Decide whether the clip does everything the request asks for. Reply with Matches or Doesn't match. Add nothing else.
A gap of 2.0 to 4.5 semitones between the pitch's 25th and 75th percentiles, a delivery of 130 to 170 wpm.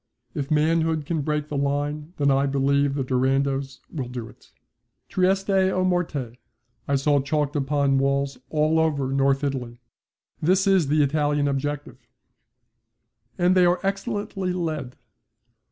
Matches